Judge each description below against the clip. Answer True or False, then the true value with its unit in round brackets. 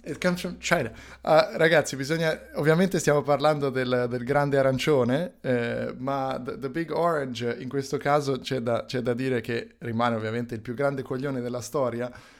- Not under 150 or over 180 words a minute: True (160 wpm)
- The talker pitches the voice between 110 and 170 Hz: True (135 Hz)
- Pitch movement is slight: False (3.6 semitones)